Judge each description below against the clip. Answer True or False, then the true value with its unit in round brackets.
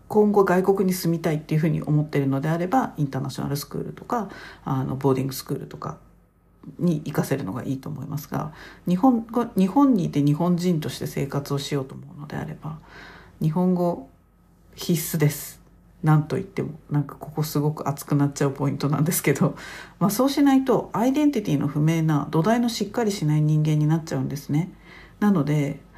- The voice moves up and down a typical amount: True (4.2 semitones)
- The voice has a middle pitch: True (155 Hz)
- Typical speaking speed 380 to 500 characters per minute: True (420 characters per minute)